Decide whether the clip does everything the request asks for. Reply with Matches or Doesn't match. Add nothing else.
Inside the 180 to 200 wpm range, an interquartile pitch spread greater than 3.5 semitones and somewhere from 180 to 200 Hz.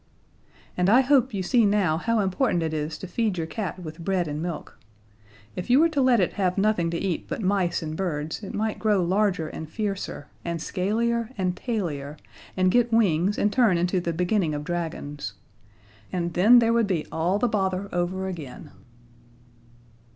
Matches